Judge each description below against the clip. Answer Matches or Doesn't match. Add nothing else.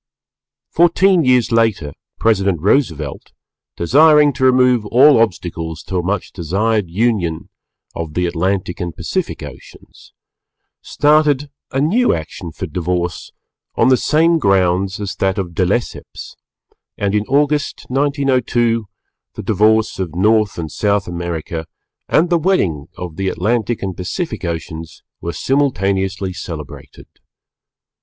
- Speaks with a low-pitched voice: Matches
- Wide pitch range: Matches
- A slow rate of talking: Matches